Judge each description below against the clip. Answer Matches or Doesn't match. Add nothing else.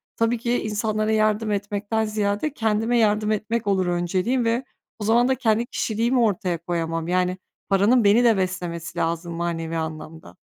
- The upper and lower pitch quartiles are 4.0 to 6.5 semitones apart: Matches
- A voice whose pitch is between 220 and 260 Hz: Doesn't match